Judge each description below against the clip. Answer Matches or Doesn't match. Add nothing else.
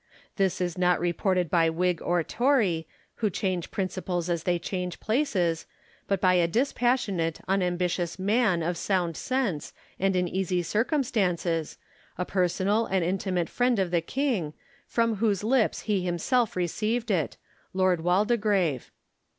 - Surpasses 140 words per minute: Matches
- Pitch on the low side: Doesn't match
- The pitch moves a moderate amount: Matches